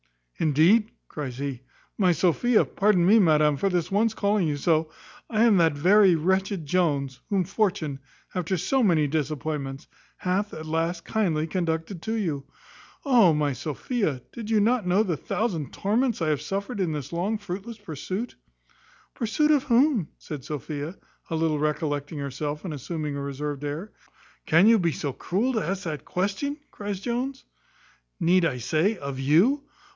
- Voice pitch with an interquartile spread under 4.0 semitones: No, wide, 5.6 semitones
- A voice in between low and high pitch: Yes, medium, 175 Hz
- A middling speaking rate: Yes, average, 160 wpm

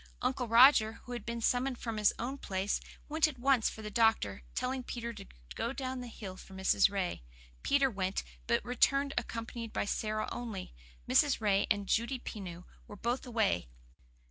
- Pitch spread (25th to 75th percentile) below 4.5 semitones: Yes, average, 3.7 semitones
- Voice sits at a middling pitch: No, high, 230 Hz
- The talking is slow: No, average, 175 wpm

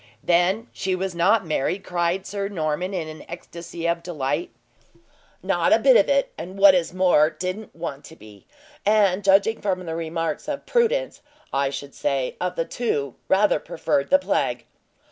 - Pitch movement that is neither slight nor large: Yes, average, 3.6 semitones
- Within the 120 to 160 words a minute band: No, average, 170 wpm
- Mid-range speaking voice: Yes, medium, 180 Hz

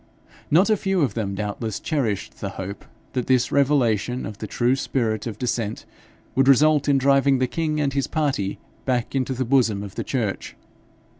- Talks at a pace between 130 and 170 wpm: No, average, 180 wpm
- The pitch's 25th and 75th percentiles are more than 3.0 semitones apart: Yes, average, 4.3 semitones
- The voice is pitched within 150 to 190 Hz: No, low, 130 Hz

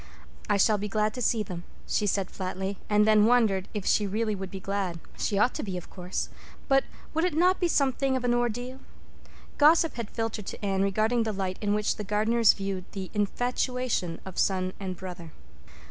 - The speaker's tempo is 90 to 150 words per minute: No, average, 200 wpm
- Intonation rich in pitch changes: No, average, 3.9 semitones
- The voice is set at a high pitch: Yes, high, 210 Hz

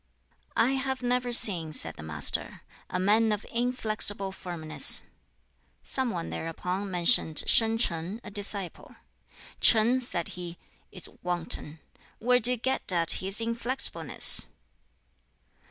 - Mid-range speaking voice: No, high, 205 Hz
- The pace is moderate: No, slow, 120 wpm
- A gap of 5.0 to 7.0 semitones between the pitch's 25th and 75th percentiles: Yes, wide, 5.6 semitones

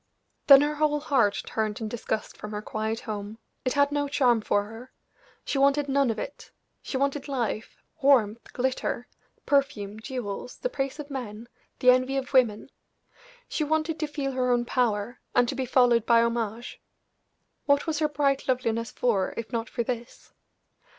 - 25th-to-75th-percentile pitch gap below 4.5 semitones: Yes, average, 3.7 semitones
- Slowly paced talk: No, average, 170 wpm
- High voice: Yes, very high, 250 Hz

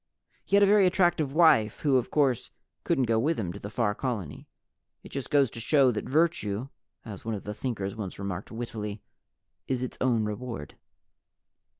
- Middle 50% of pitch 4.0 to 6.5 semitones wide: Yes, average, 5.0 semitones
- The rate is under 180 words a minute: No, average, 185 wpm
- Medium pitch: No, low, 120 Hz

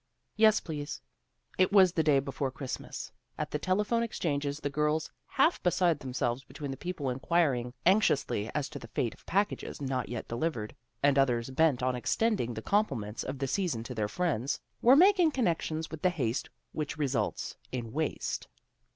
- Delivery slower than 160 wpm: No, average, 170 wpm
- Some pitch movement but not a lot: No, wide, 5.9 semitones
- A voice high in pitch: No, medium, 145 Hz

